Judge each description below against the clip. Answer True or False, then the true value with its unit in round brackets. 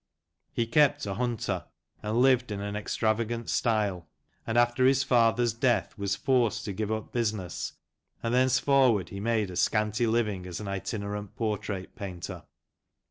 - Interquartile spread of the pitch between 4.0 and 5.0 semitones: False (2.9 semitones)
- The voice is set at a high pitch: False (110 Hz)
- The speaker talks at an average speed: True (155 wpm)